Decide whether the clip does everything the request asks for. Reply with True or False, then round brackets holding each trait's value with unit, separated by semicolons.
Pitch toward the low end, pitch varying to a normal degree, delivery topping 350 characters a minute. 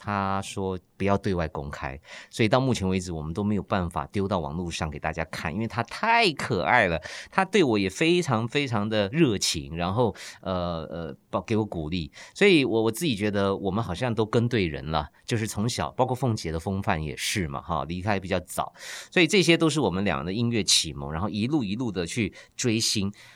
False (100 Hz; 4.9 semitones; 305 characters per minute)